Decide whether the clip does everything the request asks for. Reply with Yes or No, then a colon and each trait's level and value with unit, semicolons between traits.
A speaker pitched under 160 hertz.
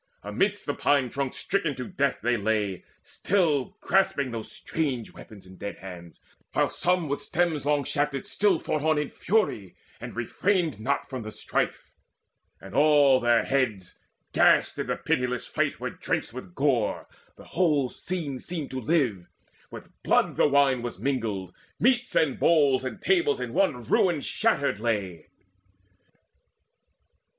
Yes: medium, 140 Hz